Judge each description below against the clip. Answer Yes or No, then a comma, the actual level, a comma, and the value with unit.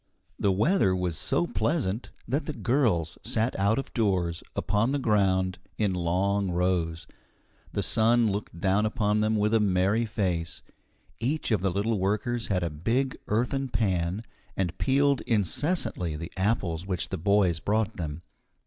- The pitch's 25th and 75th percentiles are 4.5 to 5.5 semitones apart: No, average, 4.0 semitones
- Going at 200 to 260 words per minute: No, average, 155 wpm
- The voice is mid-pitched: No, low, 100 Hz